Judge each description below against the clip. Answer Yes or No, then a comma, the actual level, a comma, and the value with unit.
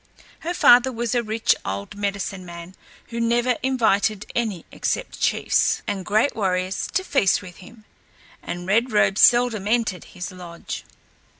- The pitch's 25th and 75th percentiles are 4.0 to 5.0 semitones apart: Yes, average, 4.4 semitones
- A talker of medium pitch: No, high, 210 Hz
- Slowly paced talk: No, average, 145 wpm